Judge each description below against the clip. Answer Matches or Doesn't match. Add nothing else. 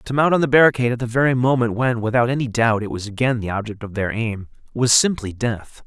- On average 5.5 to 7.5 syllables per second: Matches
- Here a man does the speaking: Matches